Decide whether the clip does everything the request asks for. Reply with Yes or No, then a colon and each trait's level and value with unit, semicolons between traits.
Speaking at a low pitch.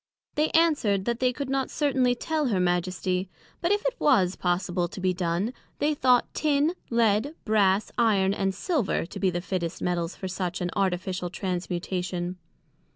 No: high, 195 Hz